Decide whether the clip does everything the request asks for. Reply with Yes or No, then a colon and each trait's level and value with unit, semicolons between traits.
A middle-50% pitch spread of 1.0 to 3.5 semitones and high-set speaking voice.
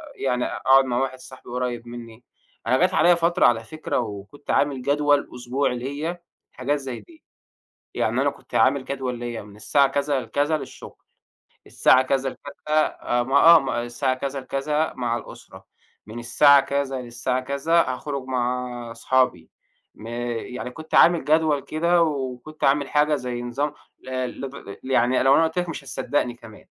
No: average, 3.0 semitones; low, 130 Hz